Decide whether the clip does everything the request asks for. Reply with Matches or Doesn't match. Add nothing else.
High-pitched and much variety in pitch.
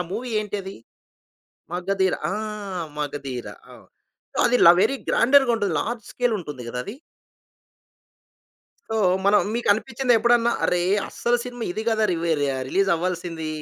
Matches